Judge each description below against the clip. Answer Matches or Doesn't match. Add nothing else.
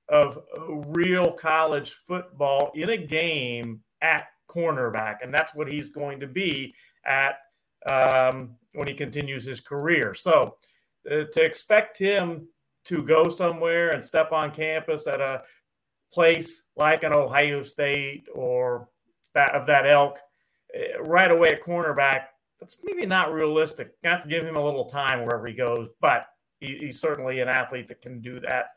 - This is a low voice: Doesn't match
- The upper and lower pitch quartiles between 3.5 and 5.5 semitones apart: Matches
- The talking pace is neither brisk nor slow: Matches